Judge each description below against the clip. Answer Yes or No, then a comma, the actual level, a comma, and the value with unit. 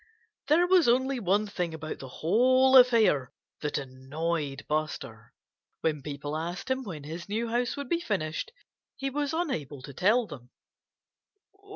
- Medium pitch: Yes, medium, 180 Hz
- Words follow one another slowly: No, average, 150 wpm